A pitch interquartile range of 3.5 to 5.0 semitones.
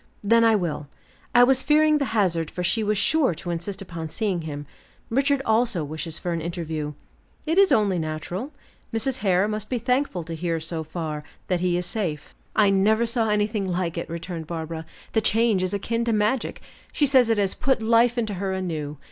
No: wide, 5.4 semitones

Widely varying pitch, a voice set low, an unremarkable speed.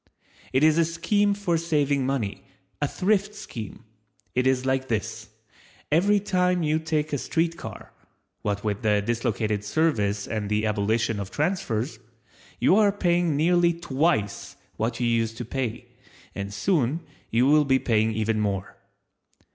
Yes: wide, 7.3 semitones; low, 130 Hz; average, 145 wpm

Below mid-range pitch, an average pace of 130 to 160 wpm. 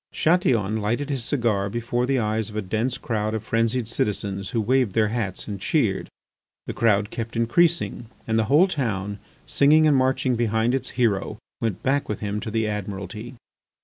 No: low, 115 Hz; average, 180 wpm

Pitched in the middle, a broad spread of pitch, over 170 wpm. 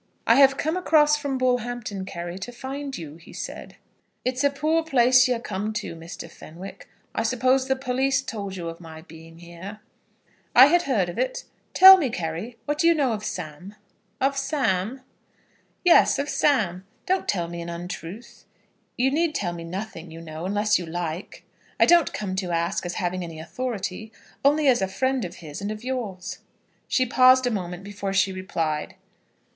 No: high, 215 Hz; wide, 7.2 semitones; average, 185 wpm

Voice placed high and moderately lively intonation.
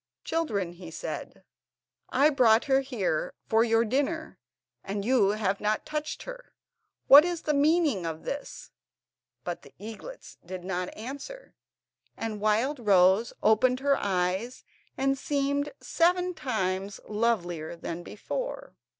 No: high, 230 Hz; wide, 6.5 semitones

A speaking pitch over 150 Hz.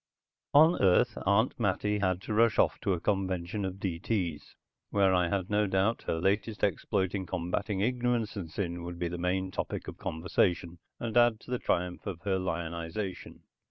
No: very low, 95 Hz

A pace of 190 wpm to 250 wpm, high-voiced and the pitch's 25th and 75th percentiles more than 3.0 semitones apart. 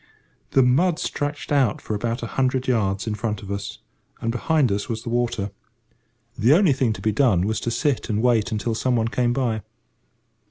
No: average, 195 wpm; low, 120 Hz; average, 3.4 semitones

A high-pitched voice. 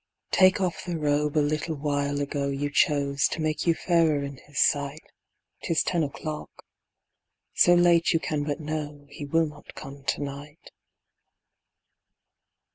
No: medium, 150 Hz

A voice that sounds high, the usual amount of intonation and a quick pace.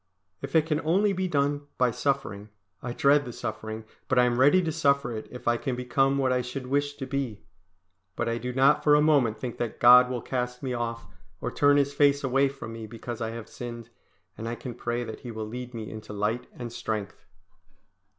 No: low, 125 Hz; average, 3.2 semitones; fast, 220 wpm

